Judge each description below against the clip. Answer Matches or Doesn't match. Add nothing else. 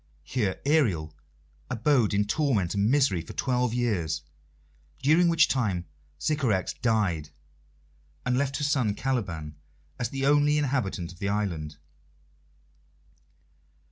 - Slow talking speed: Matches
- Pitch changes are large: Matches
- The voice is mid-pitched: Doesn't match